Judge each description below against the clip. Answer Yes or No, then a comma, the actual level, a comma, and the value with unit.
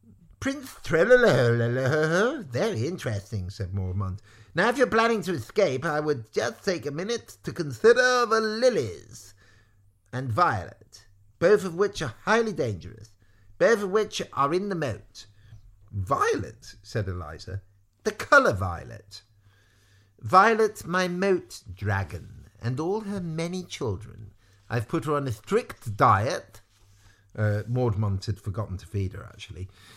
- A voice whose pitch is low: Yes, low, 110 Hz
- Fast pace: No, slow, 135 wpm